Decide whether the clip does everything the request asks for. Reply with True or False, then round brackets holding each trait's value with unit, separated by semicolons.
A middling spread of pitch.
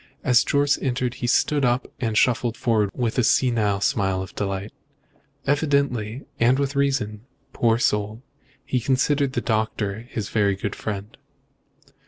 True (3.9 semitones)